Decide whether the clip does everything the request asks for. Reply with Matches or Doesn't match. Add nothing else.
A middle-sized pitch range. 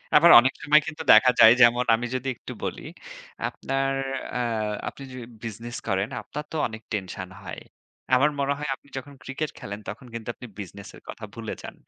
Matches